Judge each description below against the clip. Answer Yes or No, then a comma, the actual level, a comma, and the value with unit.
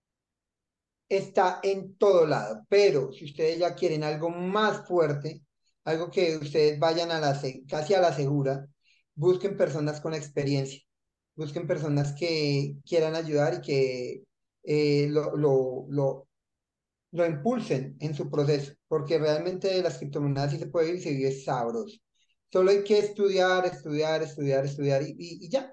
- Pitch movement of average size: Yes, average, 3.9 semitones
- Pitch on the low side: No, medium, 155 Hz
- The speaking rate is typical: Yes, average, 145 wpm